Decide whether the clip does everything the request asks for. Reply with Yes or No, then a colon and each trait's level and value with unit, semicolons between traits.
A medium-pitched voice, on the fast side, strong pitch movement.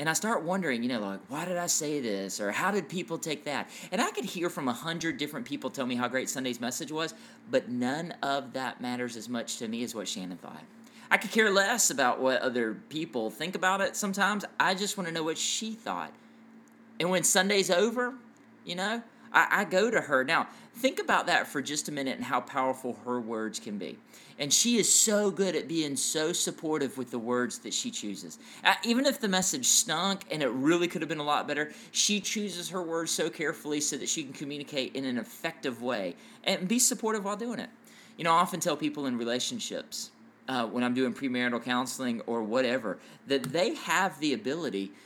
Yes: medium, 165 Hz; fast, 215 wpm; wide, 8.6 semitones